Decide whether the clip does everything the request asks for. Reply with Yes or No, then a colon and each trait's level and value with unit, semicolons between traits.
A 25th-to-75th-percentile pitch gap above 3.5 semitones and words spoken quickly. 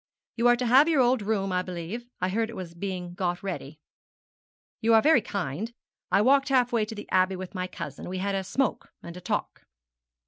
Yes: average, 4.7 semitones; fast, 215 wpm